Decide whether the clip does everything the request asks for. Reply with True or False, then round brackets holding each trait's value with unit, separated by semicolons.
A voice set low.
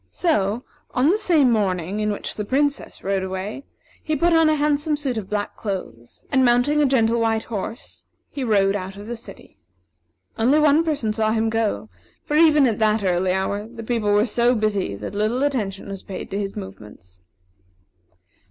False (220 Hz)